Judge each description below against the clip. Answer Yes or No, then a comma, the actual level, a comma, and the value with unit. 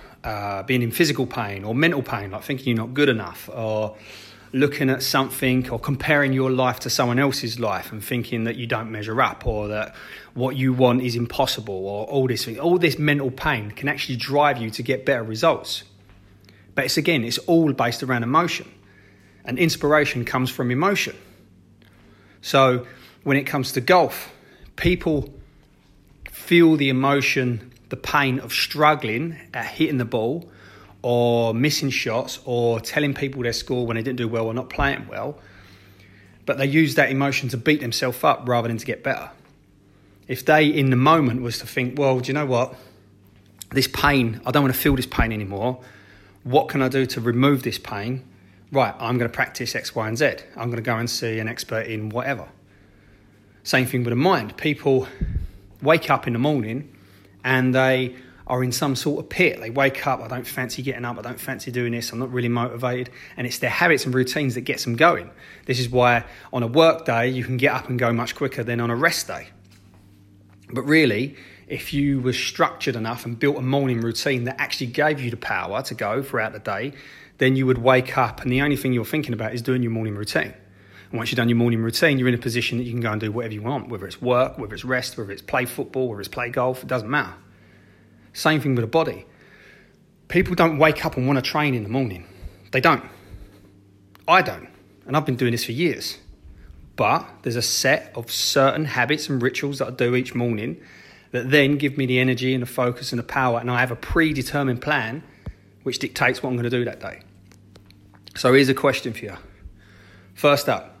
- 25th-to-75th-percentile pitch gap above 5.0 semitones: No, average, 3.6 semitones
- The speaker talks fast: Yes, fast, 210 wpm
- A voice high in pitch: No, low, 125 Hz